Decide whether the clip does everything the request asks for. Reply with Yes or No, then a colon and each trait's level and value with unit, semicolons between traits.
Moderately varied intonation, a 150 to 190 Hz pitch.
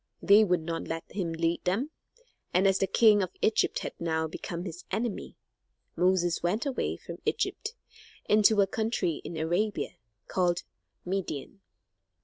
Yes: average, 3.7 semitones; medium, 185 Hz